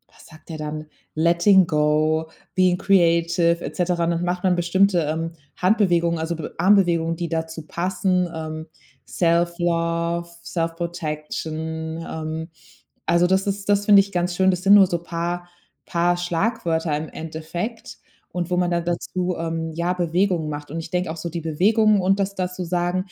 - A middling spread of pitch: No, narrow, 2.0 semitones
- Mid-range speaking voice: Yes, medium, 170 Hz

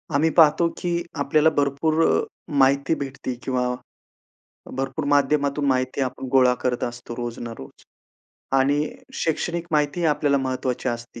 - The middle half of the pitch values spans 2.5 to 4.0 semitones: Yes, average, 2.8 semitones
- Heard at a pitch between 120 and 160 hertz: Yes, medium, 140 Hz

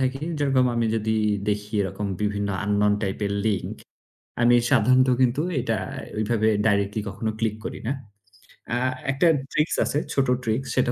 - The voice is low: Yes, low, 110 Hz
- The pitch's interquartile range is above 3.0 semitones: Yes, average, 3.9 semitones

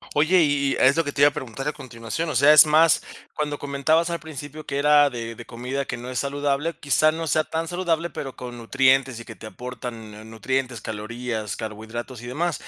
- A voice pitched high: No, medium, 140 Hz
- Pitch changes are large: No, average, 4.0 semitones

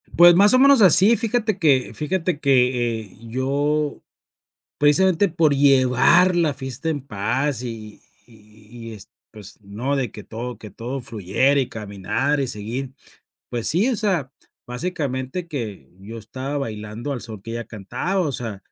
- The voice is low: Yes, low, 130 Hz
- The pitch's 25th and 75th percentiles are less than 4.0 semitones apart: No, average, 5.3 semitones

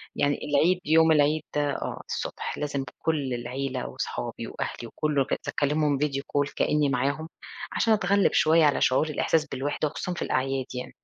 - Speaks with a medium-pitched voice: Yes, medium, 145 Hz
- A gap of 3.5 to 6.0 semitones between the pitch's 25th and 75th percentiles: No, narrow, 2.4 semitones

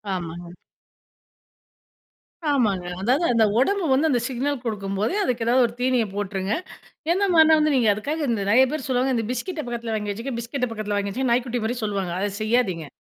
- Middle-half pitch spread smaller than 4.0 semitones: No, average, 4.3 semitones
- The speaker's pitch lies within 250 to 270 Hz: No, high, 235 Hz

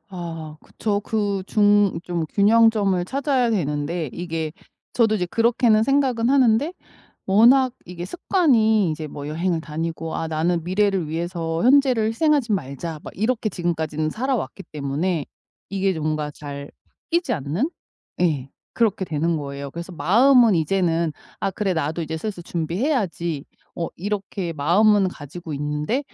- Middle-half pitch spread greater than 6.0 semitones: No, wide, 5.6 semitones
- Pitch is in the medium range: Yes, medium, 180 Hz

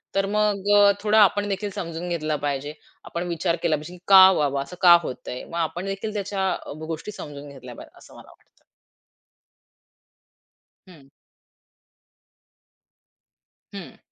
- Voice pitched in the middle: Yes, medium, 175 Hz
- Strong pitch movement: No, average, 4.4 semitones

